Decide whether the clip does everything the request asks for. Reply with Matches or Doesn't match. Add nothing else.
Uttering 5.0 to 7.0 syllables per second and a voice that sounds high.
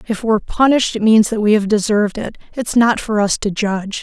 Matches